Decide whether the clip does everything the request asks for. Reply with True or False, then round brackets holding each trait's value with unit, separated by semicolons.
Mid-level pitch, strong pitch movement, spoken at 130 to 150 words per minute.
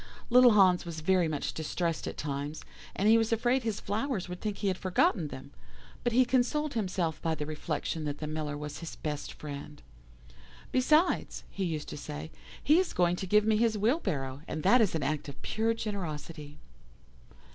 False (180 Hz; 6.6 semitones; 190 wpm)